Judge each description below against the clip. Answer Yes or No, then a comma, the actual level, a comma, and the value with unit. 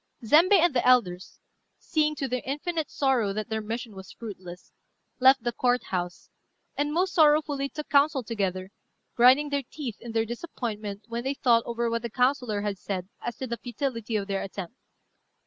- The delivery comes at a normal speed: Yes, average, 180 wpm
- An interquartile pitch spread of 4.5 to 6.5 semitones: Yes, average, 4.9 semitones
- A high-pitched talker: Yes, high, 240 Hz